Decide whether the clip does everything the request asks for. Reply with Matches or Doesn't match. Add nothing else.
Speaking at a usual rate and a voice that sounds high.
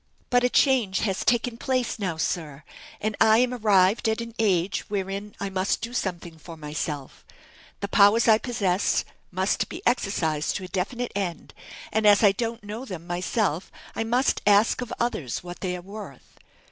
Matches